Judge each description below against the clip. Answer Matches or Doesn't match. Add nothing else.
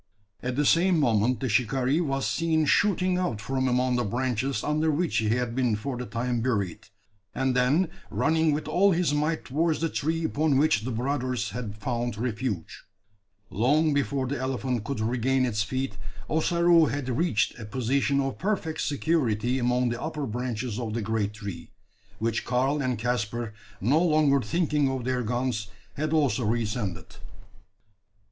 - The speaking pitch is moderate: Doesn't match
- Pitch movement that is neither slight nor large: Matches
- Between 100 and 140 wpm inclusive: Doesn't match